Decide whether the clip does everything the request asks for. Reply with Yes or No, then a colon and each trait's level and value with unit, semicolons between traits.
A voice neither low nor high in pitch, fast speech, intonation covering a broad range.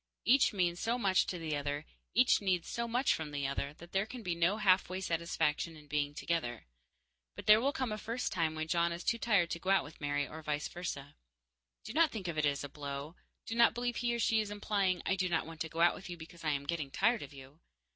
Yes: medium, 170 Hz; fast, 255 wpm; wide, 5.9 semitones